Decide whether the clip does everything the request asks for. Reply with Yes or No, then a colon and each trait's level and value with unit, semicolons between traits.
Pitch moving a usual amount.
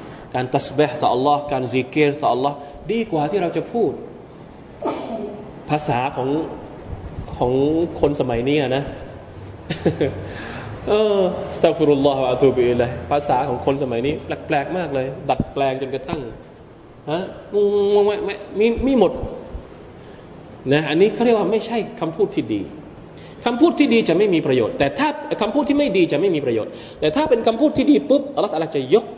No: wide, 8.3 semitones